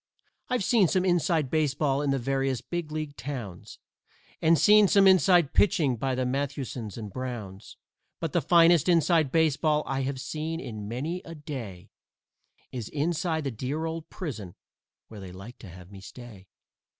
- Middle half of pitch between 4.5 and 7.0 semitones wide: Yes, average, 5.2 semitones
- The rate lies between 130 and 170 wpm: Yes, average, 160 wpm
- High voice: No, medium, 145 Hz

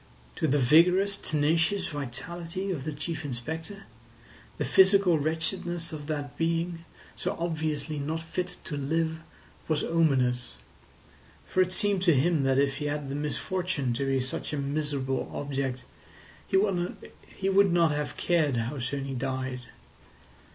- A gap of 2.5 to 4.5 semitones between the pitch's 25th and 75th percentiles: Yes, average, 3.9 semitones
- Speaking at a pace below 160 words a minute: Yes, average, 145 wpm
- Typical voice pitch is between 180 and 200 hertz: No, medium, 155 Hz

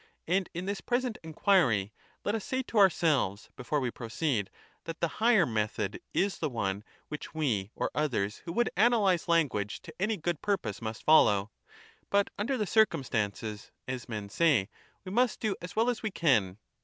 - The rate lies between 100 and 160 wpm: No, average, 175 wpm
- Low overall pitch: No, medium, 160 Hz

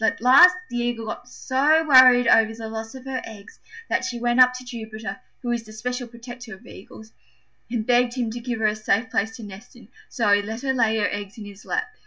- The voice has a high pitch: Yes, high, 235 Hz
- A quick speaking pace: Yes, fast, 240 wpm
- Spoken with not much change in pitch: Yes, narrow, 2.2 semitones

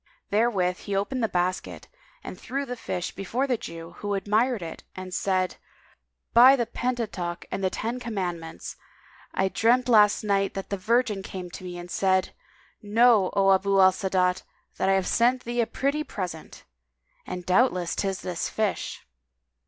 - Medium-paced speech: Yes, average, 170 wpm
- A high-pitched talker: Yes, high, 195 Hz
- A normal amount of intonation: Yes, average, 4.2 semitones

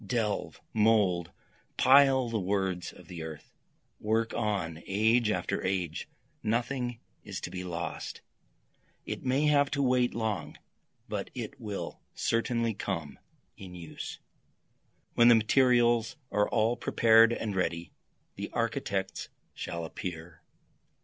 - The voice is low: Yes, low, 110 Hz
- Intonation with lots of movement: No, average, 4.6 semitones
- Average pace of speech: No, slow, 125 wpm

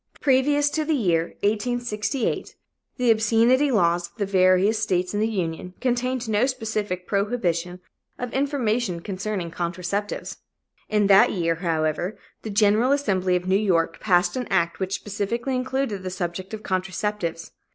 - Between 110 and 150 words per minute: Yes, average, 145 wpm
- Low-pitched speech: No, high, 205 Hz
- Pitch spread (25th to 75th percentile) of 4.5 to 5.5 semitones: Yes, average, 4.8 semitones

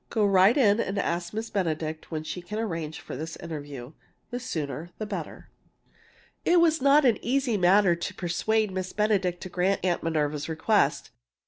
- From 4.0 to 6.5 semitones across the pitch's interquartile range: Yes, average, 4.9 semitones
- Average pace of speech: Yes, average, 175 wpm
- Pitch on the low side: No, medium, 185 Hz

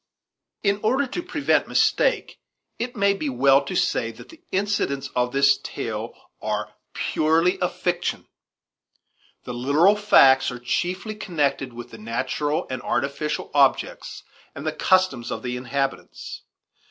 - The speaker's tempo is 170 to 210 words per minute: No, average, 140 wpm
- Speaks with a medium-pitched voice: Yes, medium, 145 Hz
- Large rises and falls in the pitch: Yes, wide, 7.5 semitones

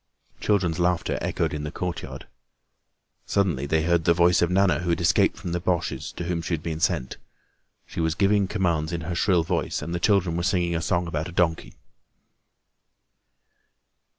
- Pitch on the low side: Yes, very low, 85 Hz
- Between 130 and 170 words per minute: No, average, 180 wpm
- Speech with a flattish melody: Yes, narrow, 1.6 semitones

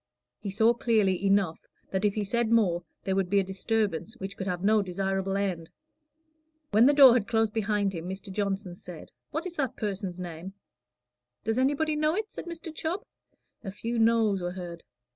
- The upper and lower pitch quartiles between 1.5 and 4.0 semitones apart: Yes, average, 3.4 semitones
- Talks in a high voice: Yes, high, 200 Hz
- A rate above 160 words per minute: Yes, average, 185 wpm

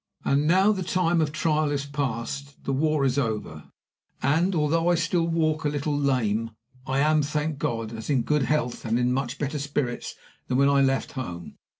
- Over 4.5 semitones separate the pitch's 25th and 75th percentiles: No, average, 3.4 semitones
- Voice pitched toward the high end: No, medium, 140 Hz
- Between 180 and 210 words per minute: Yes, average, 195 wpm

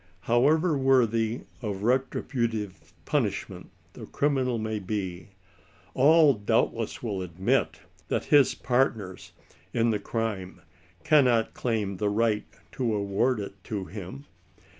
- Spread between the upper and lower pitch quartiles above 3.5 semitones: Yes, average, 4.1 semitones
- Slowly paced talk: Yes, slow, 120 wpm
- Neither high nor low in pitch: No, low, 110 Hz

